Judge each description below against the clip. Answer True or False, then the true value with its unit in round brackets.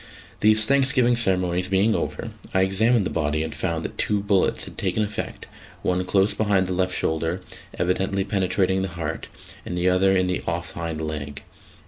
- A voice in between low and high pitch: False (95 Hz)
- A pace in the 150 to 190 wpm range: True (175 wpm)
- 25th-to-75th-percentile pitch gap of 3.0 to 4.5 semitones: False (2.6 semitones)